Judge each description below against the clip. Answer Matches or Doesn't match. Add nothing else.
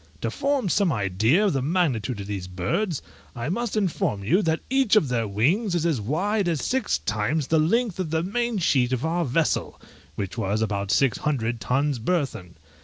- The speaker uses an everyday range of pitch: Doesn't match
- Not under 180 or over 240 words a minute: Matches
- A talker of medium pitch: Matches